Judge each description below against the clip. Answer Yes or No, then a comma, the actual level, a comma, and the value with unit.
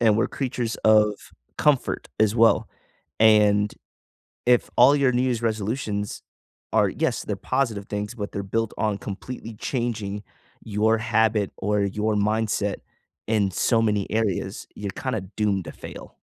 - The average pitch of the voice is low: Yes, low, 110 Hz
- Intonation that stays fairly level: Yes, narrow, 1.9 semitones